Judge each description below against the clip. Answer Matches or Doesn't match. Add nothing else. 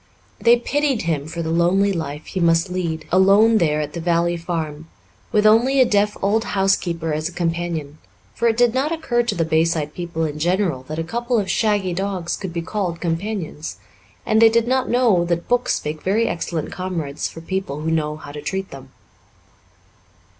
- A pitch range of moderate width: Matches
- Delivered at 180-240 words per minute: Matches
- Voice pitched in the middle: Matches